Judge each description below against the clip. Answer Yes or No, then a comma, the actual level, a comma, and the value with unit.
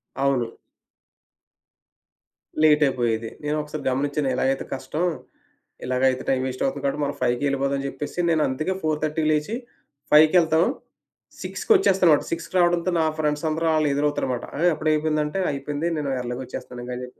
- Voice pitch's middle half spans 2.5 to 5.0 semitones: Yes, average, 2.9 semitones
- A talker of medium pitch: Yes, medium, 150 Hz